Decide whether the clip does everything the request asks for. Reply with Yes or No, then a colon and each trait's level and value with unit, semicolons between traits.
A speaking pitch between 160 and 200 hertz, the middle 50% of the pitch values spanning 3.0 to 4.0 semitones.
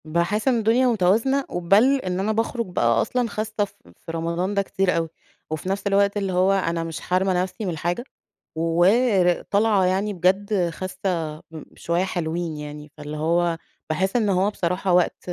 Yes: medium, 185 Hz; average, 3.3 semitones